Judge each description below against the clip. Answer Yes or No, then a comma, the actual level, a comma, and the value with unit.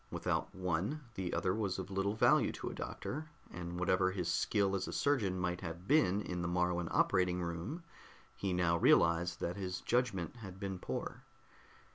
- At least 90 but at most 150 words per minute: No, average, 175 wpm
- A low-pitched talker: Yes, very low, 95 Hz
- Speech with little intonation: Yes, narrow, 2.2 semitones